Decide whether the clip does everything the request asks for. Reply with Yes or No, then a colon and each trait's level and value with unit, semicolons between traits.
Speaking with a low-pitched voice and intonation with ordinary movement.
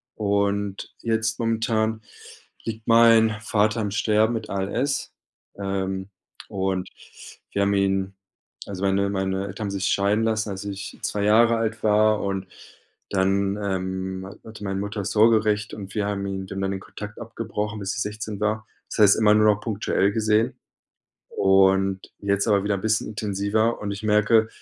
No: low, 105 Hz; narrow, 2.0 semitones